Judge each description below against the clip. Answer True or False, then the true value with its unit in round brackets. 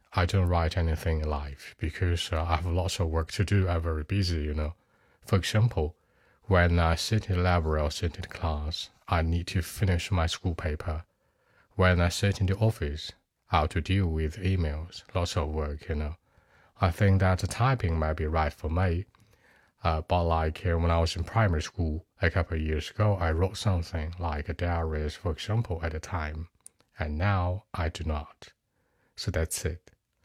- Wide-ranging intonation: False (3.1 semitones)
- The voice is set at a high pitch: False (85 Hz)